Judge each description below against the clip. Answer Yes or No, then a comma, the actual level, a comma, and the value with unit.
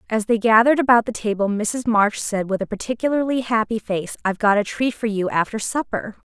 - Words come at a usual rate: No, fast, 210 wpm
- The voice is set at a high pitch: Yes, high, 220 Hz